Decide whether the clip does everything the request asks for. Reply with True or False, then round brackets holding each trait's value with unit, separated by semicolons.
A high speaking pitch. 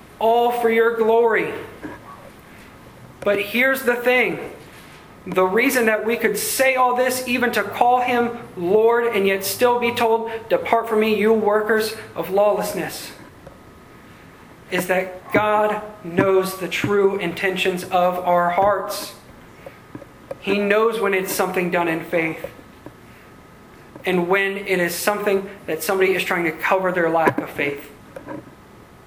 True (205 Hz)